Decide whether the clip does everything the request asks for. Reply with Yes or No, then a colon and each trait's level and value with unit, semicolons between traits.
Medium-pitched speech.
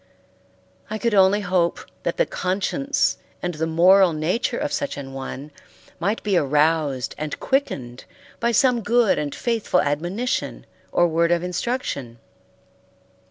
Yes: medium, 180 Hz